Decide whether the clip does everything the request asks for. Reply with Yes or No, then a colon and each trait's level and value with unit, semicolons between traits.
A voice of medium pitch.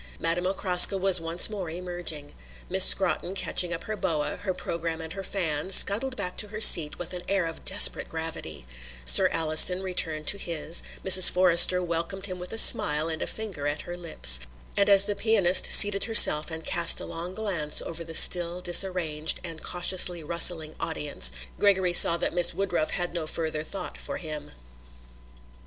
Yes: medium, 175 Hz